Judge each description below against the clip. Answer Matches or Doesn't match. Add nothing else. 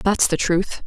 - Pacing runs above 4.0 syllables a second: Doesn't match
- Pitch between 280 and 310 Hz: Doesn't match